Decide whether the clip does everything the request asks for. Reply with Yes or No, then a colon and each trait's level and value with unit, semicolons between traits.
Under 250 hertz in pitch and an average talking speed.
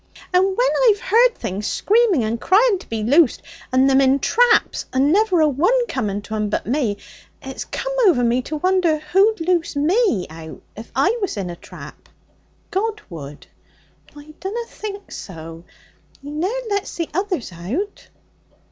No: very high, 310 Hz; average, 165 wpm